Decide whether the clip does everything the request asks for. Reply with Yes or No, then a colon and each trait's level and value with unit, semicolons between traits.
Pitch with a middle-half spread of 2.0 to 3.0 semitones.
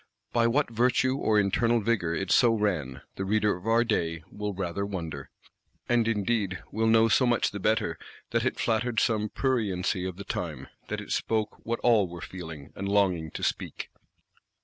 No: average, 3.9 semitones